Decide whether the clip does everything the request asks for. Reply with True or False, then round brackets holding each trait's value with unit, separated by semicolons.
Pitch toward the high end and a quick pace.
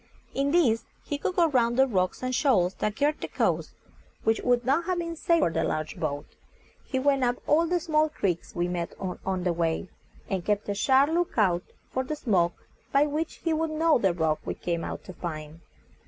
True (245 Hz; 215 wpm)